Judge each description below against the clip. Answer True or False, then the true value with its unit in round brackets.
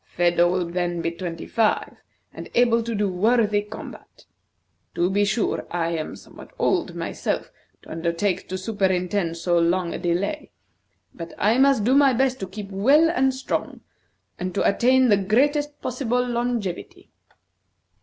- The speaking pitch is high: True (205 Hz)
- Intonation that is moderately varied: False (5.8 semitones)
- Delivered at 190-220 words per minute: False (155 wpm)